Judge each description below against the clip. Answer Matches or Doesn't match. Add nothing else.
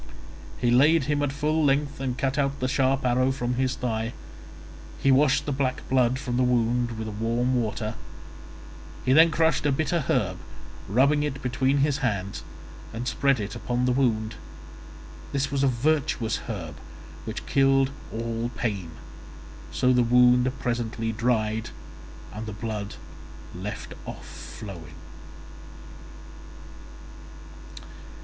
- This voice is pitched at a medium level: Doesn't match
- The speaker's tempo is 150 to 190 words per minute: Doesn't match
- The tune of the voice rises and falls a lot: Doesn't match